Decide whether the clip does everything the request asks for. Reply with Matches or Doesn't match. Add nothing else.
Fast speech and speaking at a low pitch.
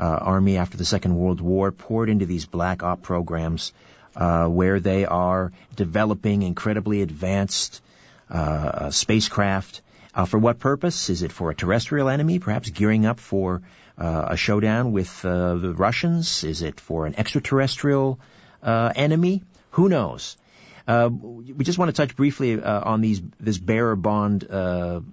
Doesn't match